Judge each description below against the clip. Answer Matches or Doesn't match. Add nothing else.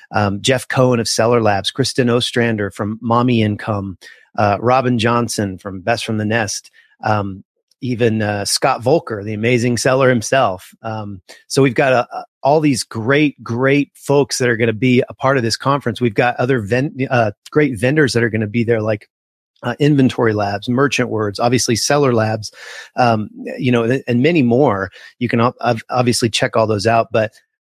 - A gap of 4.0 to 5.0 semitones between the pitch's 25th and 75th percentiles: Doesn't match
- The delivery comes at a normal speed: Matches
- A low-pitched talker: Matches